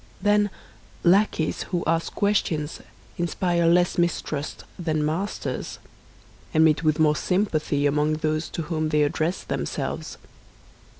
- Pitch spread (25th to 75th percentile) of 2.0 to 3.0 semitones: Yes, narrow, 2.4 semitones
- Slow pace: Yes, slow, 120 wpm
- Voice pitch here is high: No, medium, 160 Hz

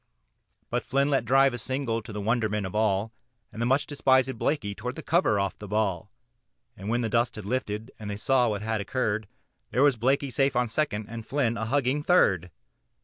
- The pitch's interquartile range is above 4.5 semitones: No, average, 4.0 semitones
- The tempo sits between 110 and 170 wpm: No, fast, 205 wpm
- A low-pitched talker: Yes, low, 115 Hz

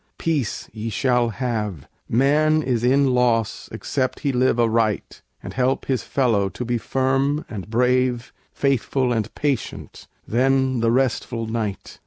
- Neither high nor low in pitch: No, low, 125 Hz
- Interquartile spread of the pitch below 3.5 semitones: Yes, average, 2.8 semitones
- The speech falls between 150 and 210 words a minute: No, average, 140 wpm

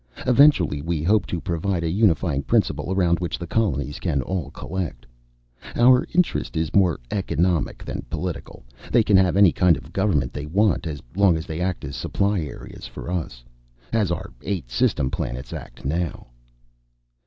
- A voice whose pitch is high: No, very low, 85 Hz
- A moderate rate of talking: Yes, average, 165 wpm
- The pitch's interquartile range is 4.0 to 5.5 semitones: Yes, average, 4.4 semitones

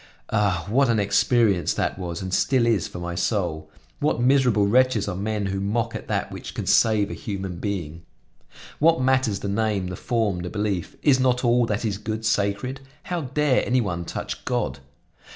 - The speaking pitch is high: No, low, 105 Hz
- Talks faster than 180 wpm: Yes, average, 190 wpm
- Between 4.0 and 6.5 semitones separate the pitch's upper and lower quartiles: Yes, average, 4.3 semitones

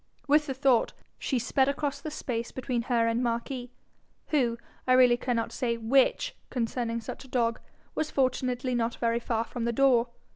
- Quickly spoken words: No, average, 175 wpm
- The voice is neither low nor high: No, high, 245 Hz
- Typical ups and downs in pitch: No, narrow, 2.2 semitones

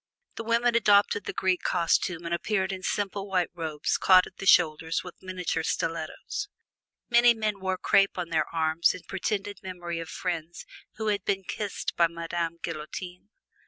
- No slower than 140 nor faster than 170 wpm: Yes, average, 165 wpm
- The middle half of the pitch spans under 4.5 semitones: Yes, average, 3.1 semitones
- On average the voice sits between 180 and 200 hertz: Yes, medium, 185 Hz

